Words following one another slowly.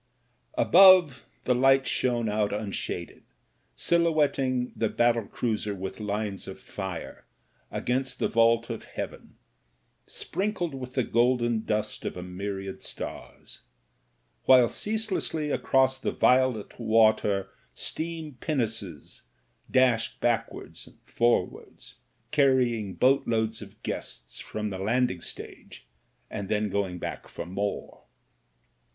Yes: slow, 115 wpm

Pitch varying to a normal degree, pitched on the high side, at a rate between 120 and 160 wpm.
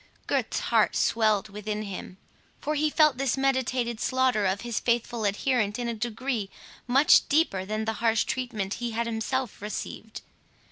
Yes: average, 3.4 semitones; high, 230 Hz; average, 155 wpm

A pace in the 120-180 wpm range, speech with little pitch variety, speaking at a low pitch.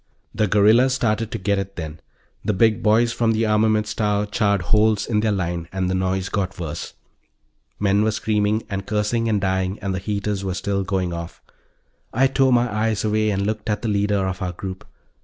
No: average, 200 wpm; narrow, 2.3 semitones; low, 105 Hz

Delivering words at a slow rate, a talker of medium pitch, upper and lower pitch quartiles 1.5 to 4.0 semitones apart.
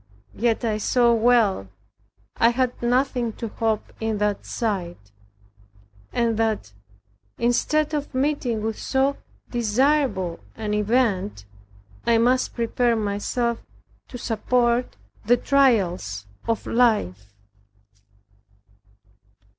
No: slow, 100 wpm; high, 230 Hz; average, 2.9 semitones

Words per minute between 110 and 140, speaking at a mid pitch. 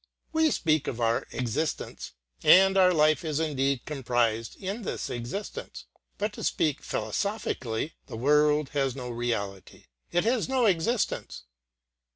Yes: slow, 135 wpm; medium, 150 Hz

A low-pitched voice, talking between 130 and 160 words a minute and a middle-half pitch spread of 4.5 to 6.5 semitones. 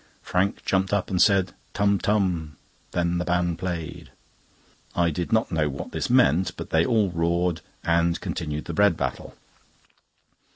No: very low, 90 Hz; average, 155 wpm; narrow, 2.4 semitones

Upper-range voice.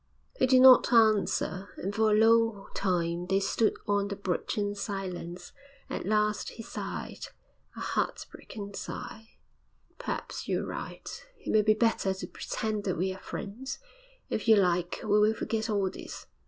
Yes: high, 205 Hz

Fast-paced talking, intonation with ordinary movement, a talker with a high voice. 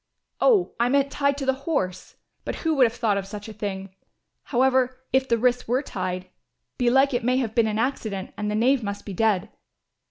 Yes: fast, 210 wpm; average, 4.2 semitones; high, 240 Hz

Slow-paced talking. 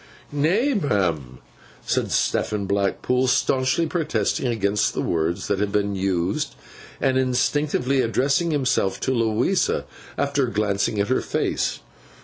Yes: slow, 125 wpm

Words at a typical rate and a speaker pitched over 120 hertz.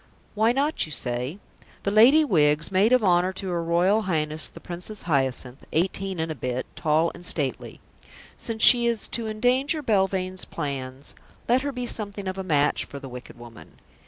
Yes: average, 180 wpm; medium, 185 Hz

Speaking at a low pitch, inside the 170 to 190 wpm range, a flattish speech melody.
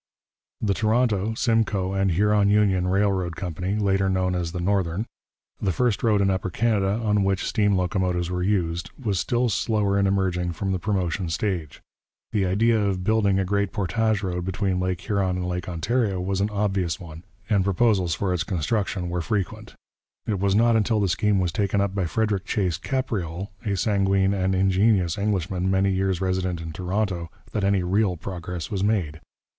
Yes: very low, 95 Hz; average, 180 wpm; narrow, 2.2 semitones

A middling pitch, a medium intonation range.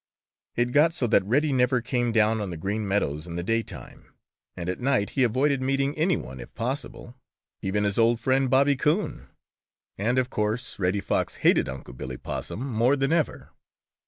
No: low, 120 Hz; average, 4.9 semitones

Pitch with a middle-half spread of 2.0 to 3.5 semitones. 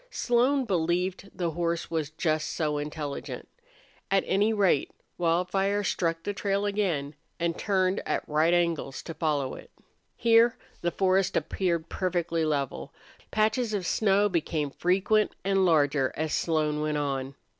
No: average, 4.1 semitones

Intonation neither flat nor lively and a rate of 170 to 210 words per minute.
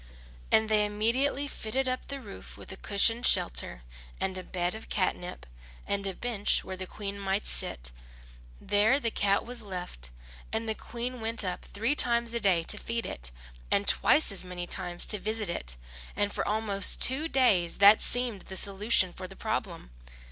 Yes: average, 3.8 semitones; average, 180 wpm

